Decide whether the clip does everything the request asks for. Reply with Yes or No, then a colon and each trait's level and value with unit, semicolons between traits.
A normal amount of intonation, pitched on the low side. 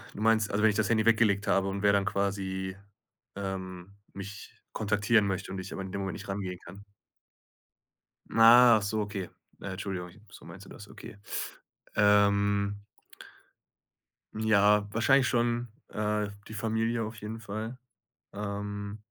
No: narrow, 1.8 semitones; low, 105 Hz